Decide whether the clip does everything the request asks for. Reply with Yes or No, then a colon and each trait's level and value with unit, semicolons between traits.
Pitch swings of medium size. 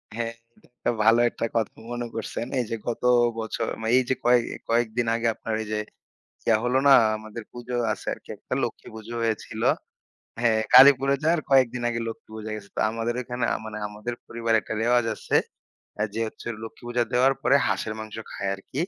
No: narrow, 1.8 semitones